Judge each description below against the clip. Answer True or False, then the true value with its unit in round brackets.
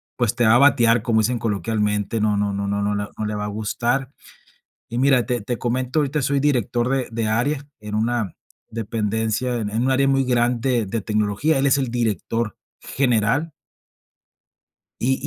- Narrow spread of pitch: False (3.3 semitones)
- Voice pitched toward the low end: True (115 Hz)